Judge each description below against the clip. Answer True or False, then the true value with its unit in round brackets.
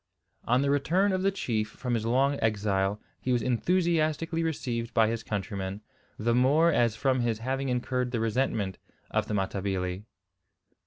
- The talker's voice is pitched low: True (120 Hz)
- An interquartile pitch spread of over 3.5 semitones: True (4.6 semitones)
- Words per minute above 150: True (160 wpm)